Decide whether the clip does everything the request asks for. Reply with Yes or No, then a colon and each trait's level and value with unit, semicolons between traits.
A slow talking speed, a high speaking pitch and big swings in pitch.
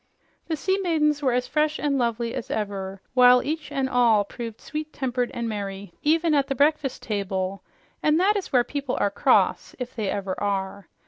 No: average, 190 wpm; very high, 250 Hz; wide, 6.6 semitones